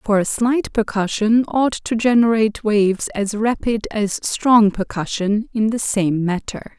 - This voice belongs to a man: No, female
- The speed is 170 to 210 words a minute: No, average, 150 wpm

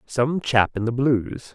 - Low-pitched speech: Yes, low, 125 Hz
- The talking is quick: No, average, 195 wpm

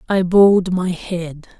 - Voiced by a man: No, female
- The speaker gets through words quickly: No, average, 150 wpm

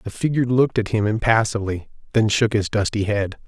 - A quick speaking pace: No, average, 190 wpm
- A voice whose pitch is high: No, low, 110 Hz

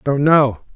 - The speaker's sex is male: Yes, male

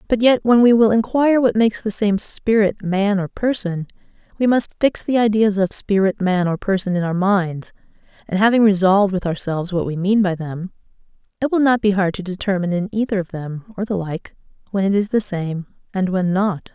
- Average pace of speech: No, fast, 210 wpm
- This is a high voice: Yes, high, 200 Hz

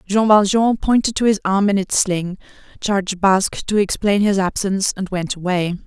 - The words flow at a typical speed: Yes, average, 185 wpm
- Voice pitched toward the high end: Yes, high, 195 Hz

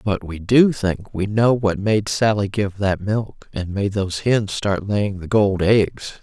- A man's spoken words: No, female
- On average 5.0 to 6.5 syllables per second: No, 3.8 syllables/s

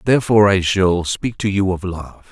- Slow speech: No, fast, 205 wpm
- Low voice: Yes, very low, 95 Hz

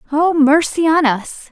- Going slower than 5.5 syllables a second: Yes, 4.0 syllables/s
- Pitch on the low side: No, very high, 300 Hz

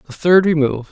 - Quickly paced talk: No, average, 195 wpm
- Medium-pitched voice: Yes, medium, 155 Hz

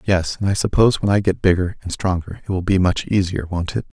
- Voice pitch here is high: No, very low, 95 Hz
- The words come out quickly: Yes, fast, 255 wpm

